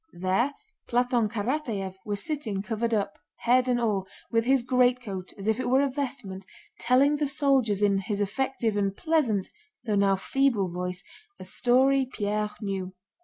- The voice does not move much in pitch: No, average, 4.6 semitones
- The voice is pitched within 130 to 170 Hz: No, high, 230 Hz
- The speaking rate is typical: Yes, average, 150 wpm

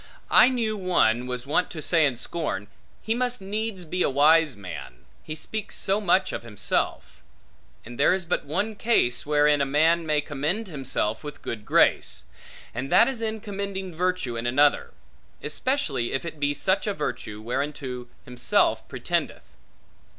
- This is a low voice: No, medium, 155 Hz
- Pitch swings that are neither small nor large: No, wide, 7.1 semitones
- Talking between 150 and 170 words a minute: Yes, average, 165 wpm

